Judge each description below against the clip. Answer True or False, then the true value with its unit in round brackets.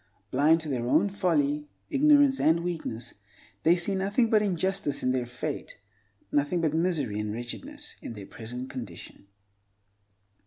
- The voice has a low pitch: False (155 Hz)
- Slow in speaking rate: False (145 wpm)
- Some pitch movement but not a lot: False (7.6 semitones)